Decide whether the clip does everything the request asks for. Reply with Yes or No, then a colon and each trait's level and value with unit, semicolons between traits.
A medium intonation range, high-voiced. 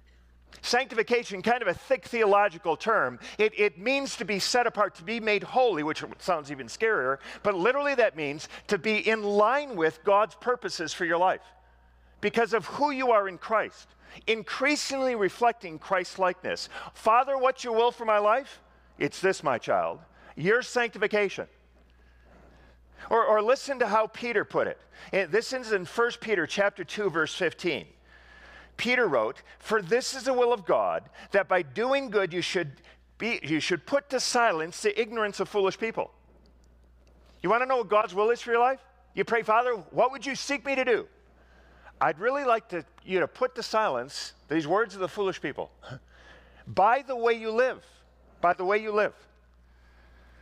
No: wide, 6.0 semitones; high, 215 Hz